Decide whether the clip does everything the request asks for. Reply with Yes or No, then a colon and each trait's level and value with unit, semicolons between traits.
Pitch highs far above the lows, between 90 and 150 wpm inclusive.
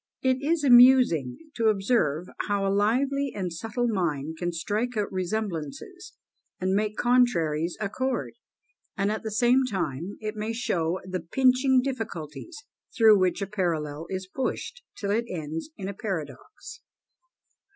Yes: wide, 6.2 semitones; average, 140 wpm